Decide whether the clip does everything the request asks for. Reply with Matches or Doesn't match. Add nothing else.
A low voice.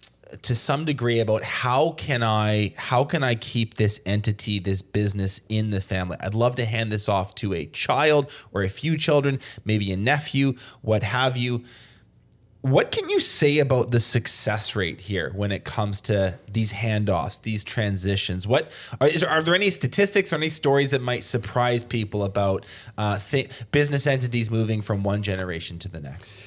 Matches